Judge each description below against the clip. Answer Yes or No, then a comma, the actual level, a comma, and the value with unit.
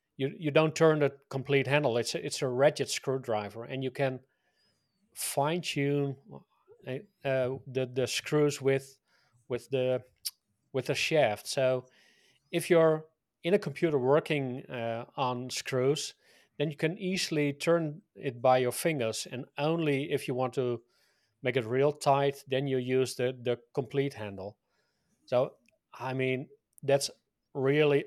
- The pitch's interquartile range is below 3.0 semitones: Yes, narrow, 2.5 semitones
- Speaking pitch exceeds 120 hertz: Yes, low, 135 Hz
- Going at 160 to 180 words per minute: No, average, 150 wpm